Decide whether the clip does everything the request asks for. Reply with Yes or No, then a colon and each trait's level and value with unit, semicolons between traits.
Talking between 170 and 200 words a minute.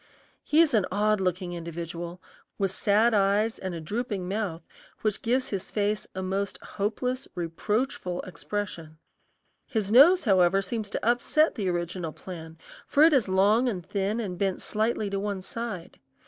No: average, 160 wpm